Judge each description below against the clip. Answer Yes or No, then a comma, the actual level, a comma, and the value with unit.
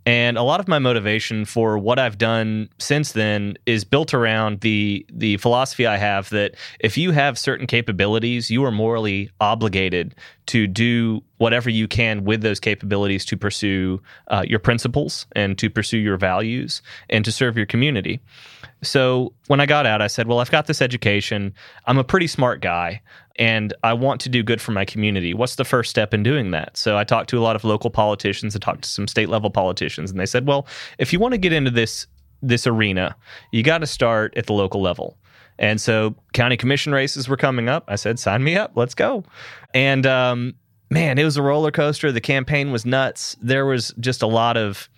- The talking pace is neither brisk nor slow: No, fast, 210 wpm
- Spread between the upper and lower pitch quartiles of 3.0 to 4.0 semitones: Yes, average, 3.7 semitones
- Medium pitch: No, low, 115 Hz